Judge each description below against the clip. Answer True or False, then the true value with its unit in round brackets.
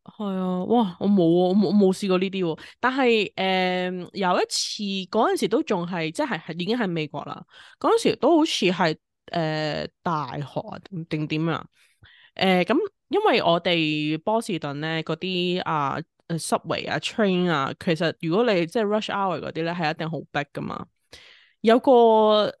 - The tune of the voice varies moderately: True (4.6 semitones)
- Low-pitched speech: False (180 Hz)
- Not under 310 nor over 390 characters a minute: False (275 characters per minute)